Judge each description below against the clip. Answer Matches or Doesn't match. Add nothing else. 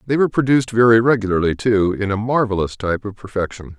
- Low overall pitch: Matches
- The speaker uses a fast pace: Doesn't match